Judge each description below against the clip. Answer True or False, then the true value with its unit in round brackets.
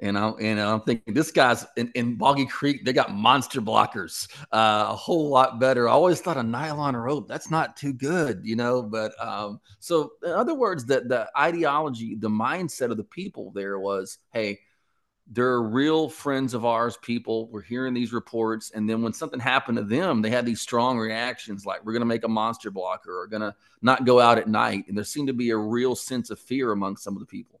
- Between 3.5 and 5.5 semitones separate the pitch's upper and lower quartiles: False (3.1 semitones)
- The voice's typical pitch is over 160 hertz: False (120 Hz)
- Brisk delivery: True (220 wpm)